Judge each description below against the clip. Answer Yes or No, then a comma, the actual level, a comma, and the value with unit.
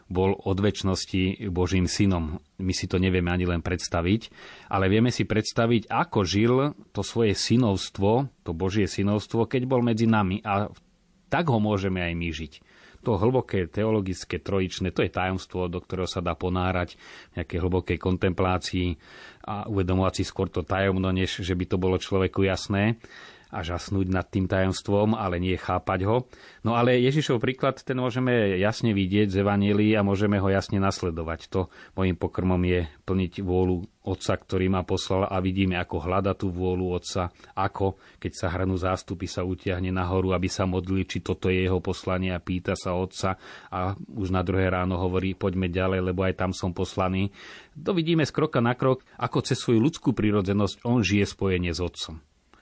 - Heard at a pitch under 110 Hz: Yes, very low, 95 Hz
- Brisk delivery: Yes, fast, 175 wpm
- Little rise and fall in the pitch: Yes, narrow, 2.3 semitones